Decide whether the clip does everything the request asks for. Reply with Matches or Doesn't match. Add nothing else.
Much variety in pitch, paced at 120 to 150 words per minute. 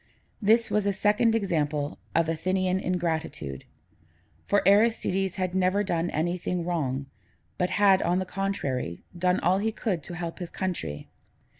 Doesn't match